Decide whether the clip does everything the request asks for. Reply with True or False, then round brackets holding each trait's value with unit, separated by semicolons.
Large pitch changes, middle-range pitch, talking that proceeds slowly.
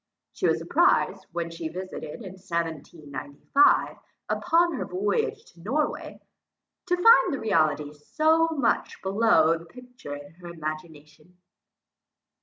True (8.1 semitones; 175 Hz; 130 wpm)